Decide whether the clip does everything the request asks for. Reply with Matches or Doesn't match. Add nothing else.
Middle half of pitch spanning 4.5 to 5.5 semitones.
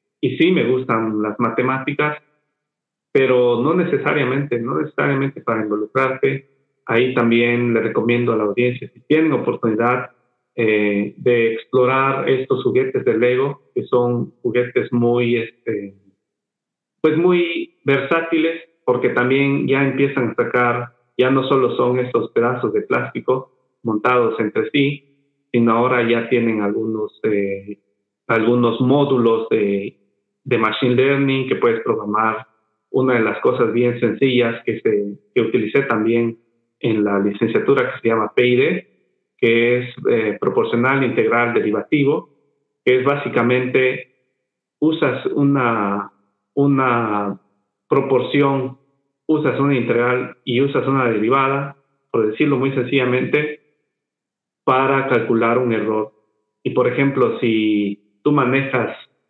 Doesn't match